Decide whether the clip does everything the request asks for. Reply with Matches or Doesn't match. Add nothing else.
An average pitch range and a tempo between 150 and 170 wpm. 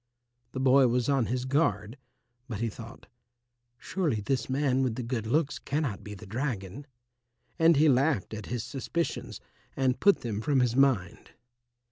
Matches